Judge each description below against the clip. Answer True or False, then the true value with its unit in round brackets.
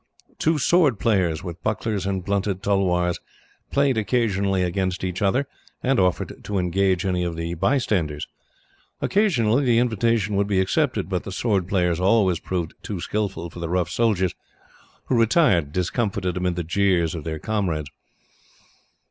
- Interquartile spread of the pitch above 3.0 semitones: True (3.9 semitones)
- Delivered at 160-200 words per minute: False (150 wpm)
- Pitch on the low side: True (95 Hz)